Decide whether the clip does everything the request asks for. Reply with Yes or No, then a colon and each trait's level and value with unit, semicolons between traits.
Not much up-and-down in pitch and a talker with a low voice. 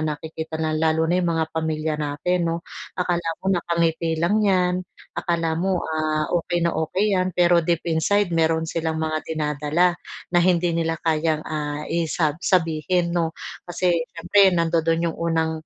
No: narrow, 1.7 semitones; medium, 165 Hz